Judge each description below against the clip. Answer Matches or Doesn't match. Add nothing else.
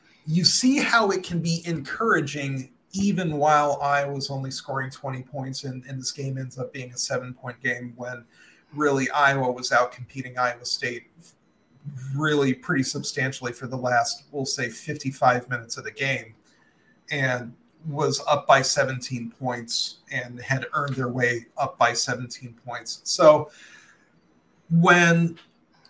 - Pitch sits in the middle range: Doesn't match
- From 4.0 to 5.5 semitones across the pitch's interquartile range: Doesn't match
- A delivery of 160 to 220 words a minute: Doesn't match